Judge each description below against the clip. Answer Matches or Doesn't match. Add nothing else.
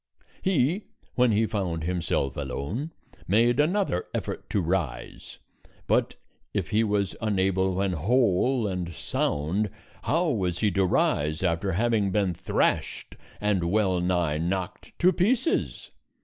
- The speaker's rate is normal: Doesn't match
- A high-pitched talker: Doesn't match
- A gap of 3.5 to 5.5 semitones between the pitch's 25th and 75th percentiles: Matches